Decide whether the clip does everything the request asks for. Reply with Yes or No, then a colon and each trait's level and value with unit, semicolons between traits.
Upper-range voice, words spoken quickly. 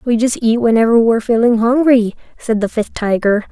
No: high, 230 Hz; average, 190 wpm